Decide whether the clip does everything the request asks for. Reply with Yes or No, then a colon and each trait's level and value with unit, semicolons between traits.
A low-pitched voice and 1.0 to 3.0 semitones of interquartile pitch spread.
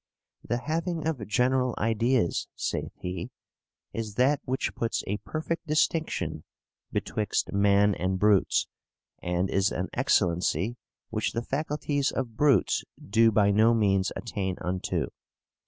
No: low, 110 Hz; average, 5.3 semitones